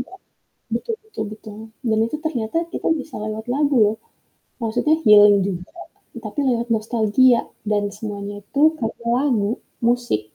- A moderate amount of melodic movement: Yes, average, 3.4 semitones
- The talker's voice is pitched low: No, high, 225 Hz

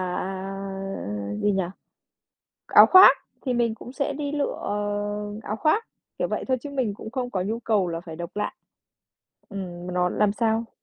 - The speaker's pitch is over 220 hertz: No, high, 205 Hz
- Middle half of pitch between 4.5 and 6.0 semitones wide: No, average, 4.1 semitones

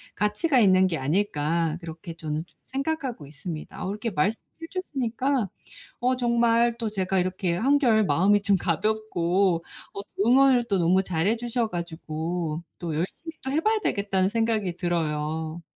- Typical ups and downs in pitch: No, wide, 5.8 semitones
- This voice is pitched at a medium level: No, high, 195 Hz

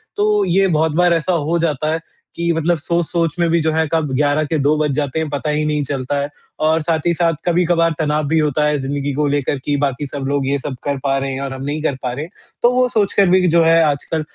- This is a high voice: No, medium, 155 Hz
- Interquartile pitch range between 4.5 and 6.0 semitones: No, average, 2.8 semitones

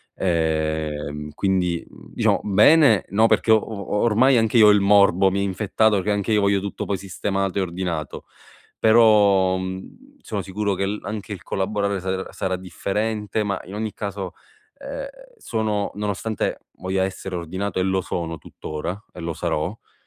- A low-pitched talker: Yes, low, 100 Hz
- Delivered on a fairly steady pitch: Yes, narrow, 2.2 semitones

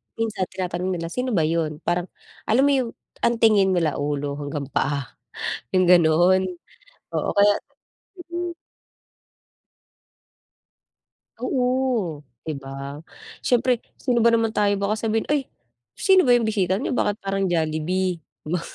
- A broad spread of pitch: Yes, wide, 6.1 semitones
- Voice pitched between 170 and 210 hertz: Yes, high, 190 Hz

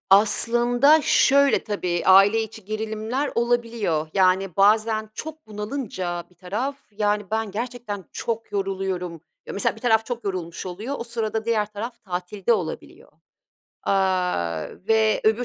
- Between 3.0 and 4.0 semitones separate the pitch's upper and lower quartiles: Yes, average, 3.4 semitones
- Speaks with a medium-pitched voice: No, high, 215 Hz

